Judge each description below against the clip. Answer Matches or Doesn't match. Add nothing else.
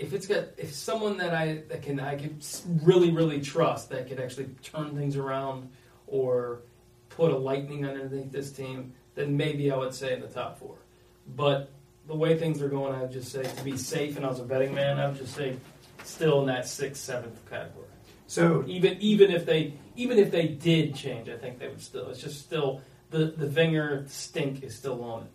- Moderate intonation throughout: Matches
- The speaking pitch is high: Doesn't match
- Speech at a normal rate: Doesn't match